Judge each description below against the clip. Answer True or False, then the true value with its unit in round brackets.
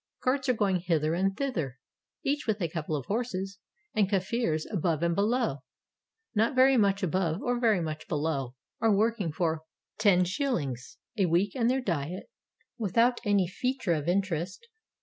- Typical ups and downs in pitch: False (5.9 semitones)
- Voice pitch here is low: False (195 Hz)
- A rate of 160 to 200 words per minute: True (170 wpm)